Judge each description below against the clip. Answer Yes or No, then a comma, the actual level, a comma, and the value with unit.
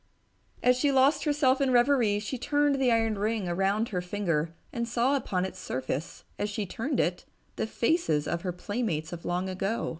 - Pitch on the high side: Yes, high, 215 Hz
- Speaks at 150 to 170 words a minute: No, average, 185 wpm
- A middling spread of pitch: No, wide, 6.0 semitones